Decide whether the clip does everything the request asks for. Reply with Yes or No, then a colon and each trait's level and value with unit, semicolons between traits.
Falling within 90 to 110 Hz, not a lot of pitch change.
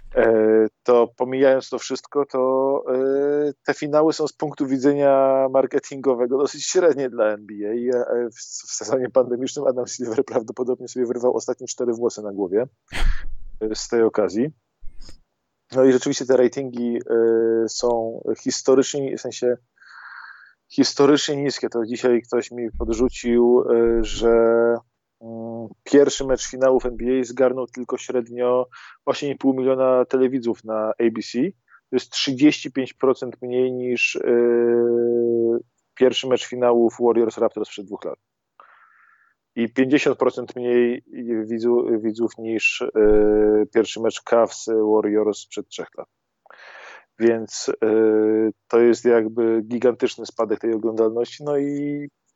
No: low, 120 Hz; narrow, 2.3 semitones